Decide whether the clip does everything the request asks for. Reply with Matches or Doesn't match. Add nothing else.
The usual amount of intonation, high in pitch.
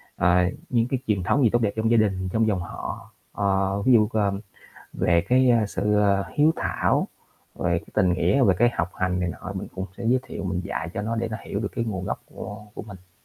Doesn't match